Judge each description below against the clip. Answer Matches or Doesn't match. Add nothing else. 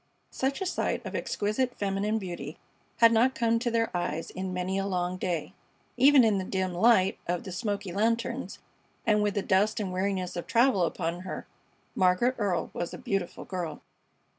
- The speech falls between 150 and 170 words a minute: Doesn't match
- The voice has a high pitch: Matches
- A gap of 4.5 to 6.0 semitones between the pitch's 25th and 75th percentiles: Doesn't match